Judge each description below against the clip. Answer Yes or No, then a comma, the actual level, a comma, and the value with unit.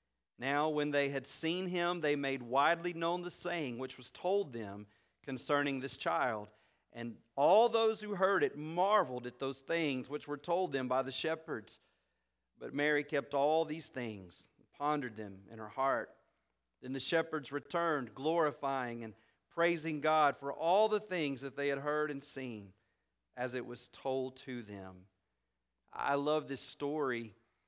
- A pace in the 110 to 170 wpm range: Yes, average, 165 wpm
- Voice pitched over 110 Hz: Yes, medium, 140 Hz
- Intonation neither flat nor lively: Yes, average, 5.0 semitones